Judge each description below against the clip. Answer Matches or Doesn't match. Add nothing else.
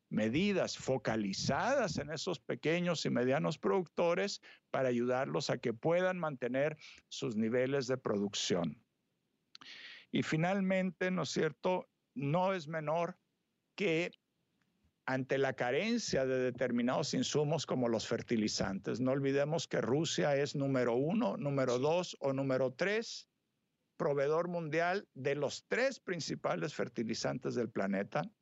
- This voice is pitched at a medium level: Matches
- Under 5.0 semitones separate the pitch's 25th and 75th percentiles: Doesn't match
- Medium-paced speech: Doesn't match